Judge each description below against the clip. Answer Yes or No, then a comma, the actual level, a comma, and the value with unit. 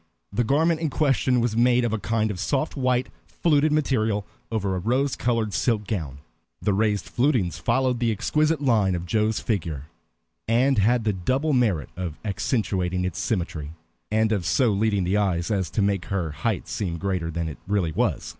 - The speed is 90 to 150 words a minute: No, average, 185 wpm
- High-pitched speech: No, low, 110 Hz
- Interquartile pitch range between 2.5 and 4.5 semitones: No, average, 5.1 semitones